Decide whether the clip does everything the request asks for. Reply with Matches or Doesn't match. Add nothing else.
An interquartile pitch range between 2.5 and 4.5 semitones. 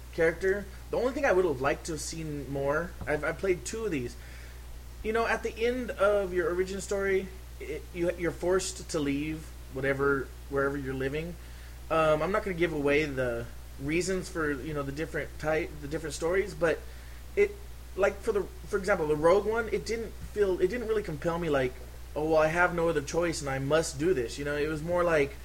Doesn't match